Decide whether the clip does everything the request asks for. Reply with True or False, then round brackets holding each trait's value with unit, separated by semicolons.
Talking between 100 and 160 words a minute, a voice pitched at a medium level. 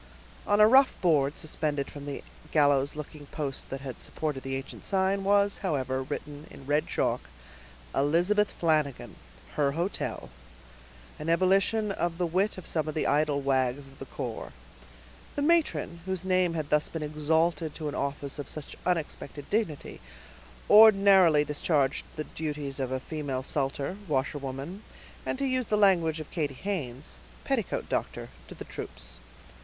True (155 wpm; 155 Hz)